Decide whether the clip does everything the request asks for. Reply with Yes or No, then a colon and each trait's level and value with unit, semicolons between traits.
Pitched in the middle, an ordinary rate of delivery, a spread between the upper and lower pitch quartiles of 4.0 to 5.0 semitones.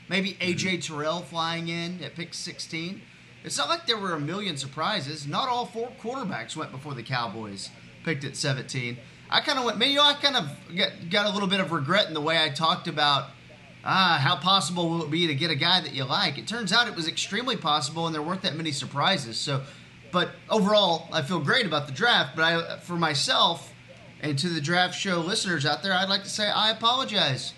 No: medium, 165 Hz; fast, 220 wpm; average, 4.6 semitones